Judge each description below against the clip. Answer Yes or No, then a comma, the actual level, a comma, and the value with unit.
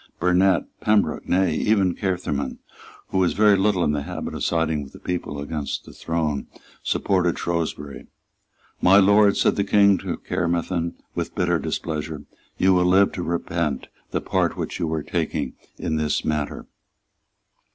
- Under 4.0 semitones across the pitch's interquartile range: Yes, average, 3.5 semitones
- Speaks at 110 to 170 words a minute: Yes, average, 155 wpm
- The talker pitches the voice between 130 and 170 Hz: No, very low, 85 Hz